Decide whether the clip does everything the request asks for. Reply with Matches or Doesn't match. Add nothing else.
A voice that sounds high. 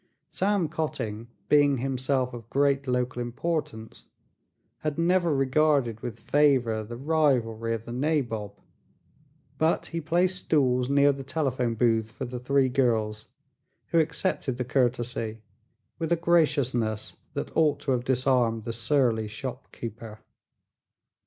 Doesn't match